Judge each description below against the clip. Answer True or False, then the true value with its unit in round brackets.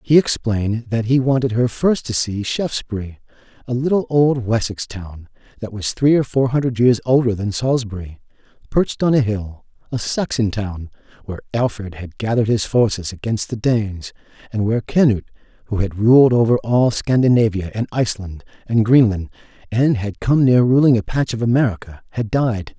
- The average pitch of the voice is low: True (115 Hz)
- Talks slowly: False (170 wpm)